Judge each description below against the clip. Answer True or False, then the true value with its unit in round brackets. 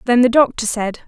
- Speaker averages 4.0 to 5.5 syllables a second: False (5.7 syllables/s)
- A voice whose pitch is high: True (235 Hz)